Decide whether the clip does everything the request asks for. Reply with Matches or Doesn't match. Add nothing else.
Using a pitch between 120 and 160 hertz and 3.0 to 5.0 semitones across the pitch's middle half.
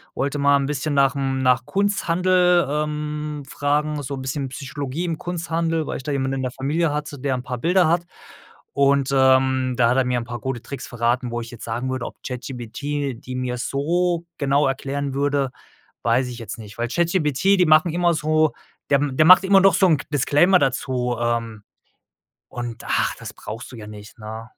Matches